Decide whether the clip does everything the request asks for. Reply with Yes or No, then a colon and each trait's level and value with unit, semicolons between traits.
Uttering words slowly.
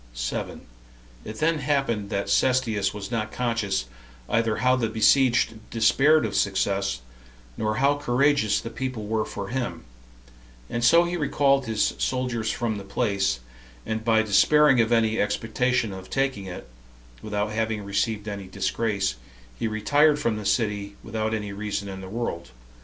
No: average, 150 wpm